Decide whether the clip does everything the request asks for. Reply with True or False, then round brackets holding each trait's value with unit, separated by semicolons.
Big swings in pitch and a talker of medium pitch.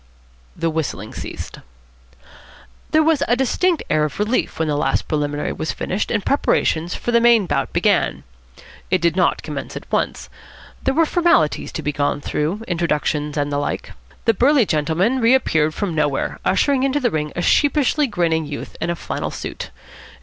True (8.6 semitones; 175 Hz)